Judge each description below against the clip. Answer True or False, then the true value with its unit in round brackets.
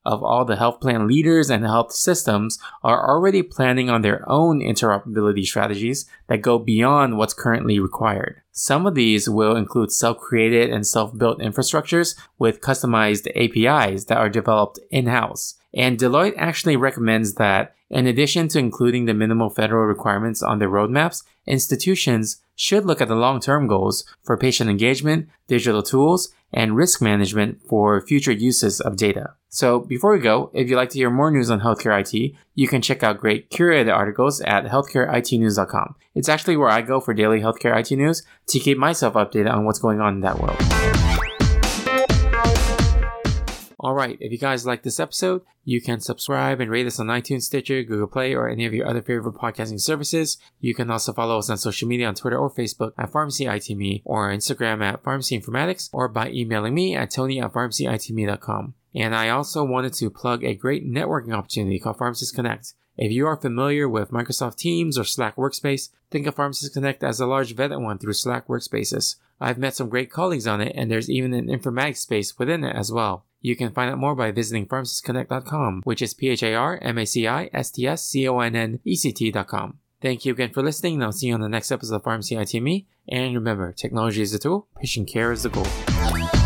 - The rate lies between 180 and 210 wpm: True (185 wpm)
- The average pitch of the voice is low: True (120 Hz)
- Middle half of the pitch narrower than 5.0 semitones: True (3.6 semitones)